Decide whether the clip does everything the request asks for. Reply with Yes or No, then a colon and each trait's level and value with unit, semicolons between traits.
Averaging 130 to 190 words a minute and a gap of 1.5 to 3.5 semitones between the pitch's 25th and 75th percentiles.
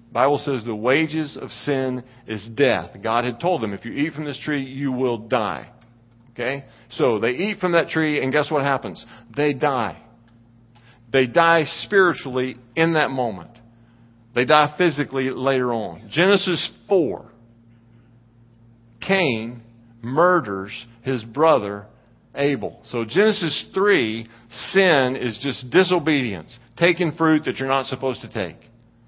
No: average, 140 wpm; average, 4.4 semitones